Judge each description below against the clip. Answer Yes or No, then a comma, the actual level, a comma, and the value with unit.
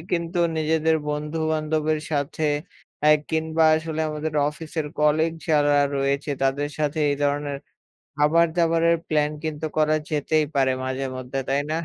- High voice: No, medium, 155 Hz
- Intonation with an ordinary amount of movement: No, narrow, 1.6 semitones